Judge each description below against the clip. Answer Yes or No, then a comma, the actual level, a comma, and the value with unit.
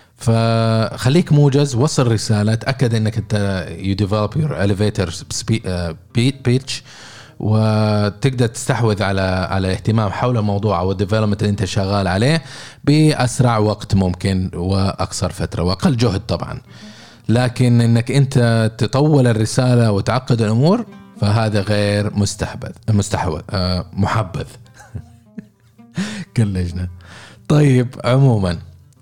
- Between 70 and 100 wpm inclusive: Yes, average, 90 wpm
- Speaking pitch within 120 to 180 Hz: No, low, 110 Hz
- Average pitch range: Yes, average, 3.9 semitones